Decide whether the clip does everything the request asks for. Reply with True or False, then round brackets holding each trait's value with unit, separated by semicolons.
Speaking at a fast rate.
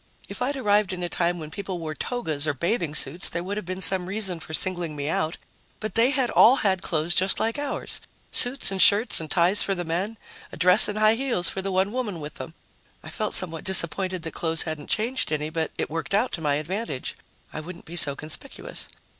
True (225 wpm)